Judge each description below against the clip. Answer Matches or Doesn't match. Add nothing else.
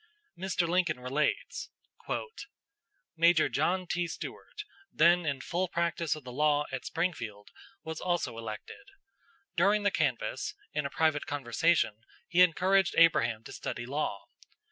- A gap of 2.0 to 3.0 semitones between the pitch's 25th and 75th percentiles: Doesn't match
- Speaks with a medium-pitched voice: Matches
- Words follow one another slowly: Matches